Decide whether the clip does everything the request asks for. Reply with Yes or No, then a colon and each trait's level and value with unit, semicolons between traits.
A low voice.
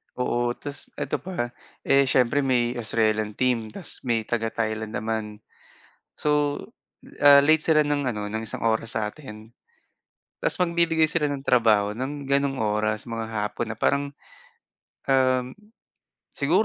Yes: low, 125 Hz